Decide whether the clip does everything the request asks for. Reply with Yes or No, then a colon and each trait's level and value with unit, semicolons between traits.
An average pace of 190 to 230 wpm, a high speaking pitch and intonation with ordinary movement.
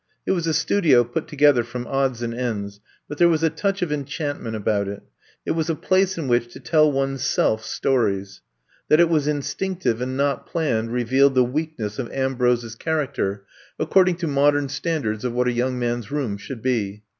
No: average, 200 wpm; low, 135 Hz; average, 4.4 semitones